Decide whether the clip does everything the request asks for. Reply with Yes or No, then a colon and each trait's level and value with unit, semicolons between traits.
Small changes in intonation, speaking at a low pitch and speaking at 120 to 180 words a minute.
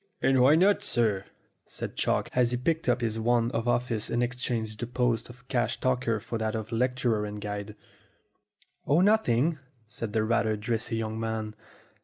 Yes: narrow, 2.2 semitones; low, 115 Hz; average, 175 wpm